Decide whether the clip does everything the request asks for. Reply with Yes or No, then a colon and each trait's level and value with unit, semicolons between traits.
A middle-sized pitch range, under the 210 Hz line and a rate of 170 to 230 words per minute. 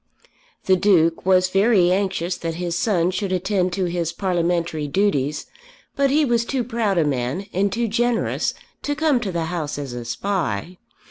Yes: average, 3.7 semitones; medium, 185 Hz; average, 175 wpm